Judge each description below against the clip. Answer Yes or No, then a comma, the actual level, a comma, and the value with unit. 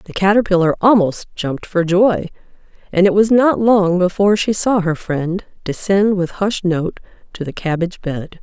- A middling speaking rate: Yes, average, 170 wpm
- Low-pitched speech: No, medium, 185 Hz